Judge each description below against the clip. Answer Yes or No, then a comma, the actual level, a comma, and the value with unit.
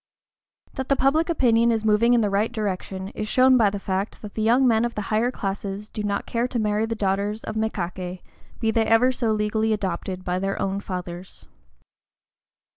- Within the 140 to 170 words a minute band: No, average, 195 wpm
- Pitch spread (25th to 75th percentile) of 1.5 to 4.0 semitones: Yes, average, 2.8 semitones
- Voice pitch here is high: Yes, high, 215 Hz